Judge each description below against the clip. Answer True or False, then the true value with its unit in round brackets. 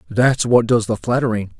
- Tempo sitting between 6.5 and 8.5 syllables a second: False (5.0 syllables/s)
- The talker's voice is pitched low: True (115 Hz)